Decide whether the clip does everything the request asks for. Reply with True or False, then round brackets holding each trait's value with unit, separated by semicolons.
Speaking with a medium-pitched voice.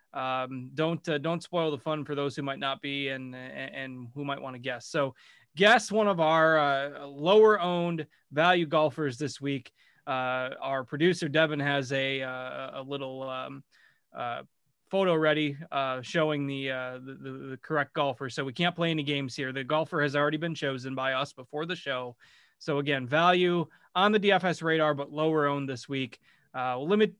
True (145 Hz)